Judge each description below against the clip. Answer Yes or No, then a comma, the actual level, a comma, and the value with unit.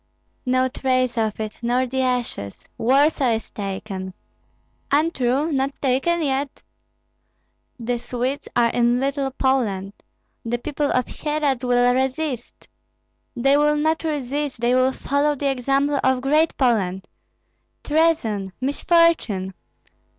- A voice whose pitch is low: No, very high, 260 Hz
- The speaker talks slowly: Yes, slow, 120 wpm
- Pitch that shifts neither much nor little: Yes, average, 3.2 semitones